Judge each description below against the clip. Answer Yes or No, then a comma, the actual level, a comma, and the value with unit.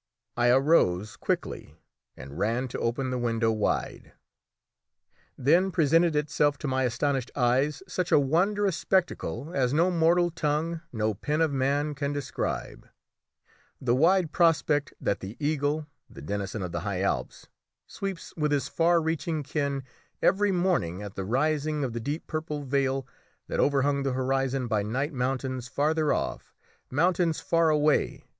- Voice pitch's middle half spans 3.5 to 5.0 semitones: Yes, average, 4.2 semitones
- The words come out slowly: No, average, 150 wpm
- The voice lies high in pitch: No, medium, 145 Hz